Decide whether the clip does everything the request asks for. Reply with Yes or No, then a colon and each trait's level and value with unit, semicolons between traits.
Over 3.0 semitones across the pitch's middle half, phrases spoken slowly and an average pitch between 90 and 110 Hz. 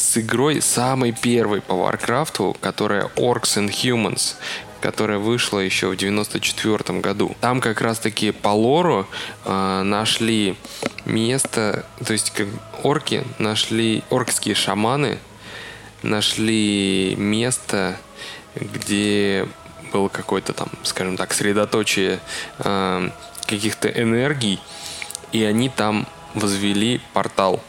No: narrow, 2.4 semitones; slow, 105 wpm; low, 105 Hz